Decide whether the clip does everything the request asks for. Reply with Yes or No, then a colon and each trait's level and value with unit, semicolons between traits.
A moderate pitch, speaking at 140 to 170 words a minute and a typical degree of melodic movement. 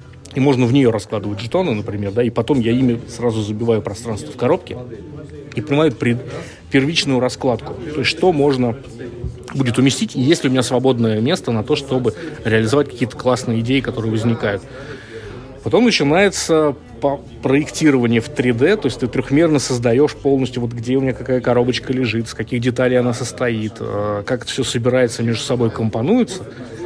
No: low, 125 Hz; fast, 160 wpm; average, 3.0 semitones